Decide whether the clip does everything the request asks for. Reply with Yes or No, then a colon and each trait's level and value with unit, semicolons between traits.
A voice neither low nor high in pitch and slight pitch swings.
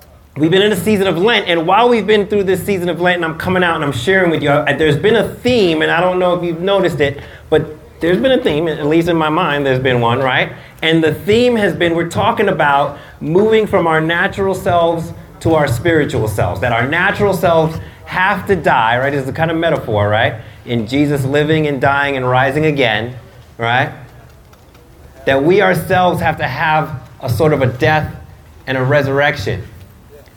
No: medium, 155 Hz; average, 5.2 semitones